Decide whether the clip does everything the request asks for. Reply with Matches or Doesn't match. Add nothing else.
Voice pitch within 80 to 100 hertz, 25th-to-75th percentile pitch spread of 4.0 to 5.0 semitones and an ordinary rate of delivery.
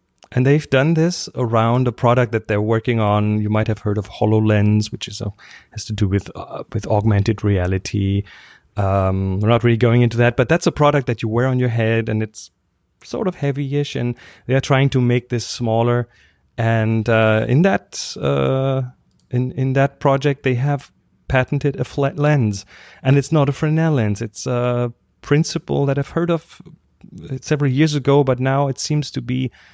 Doesn't match